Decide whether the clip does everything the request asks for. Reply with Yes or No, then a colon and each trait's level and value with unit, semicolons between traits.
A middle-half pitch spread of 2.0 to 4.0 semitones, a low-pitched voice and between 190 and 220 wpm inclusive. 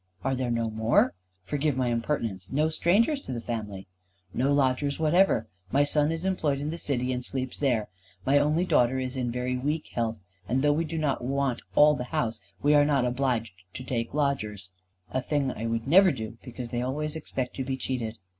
Yes: average, 3.7 semitones; low, 130 Hz; average, 200 wpm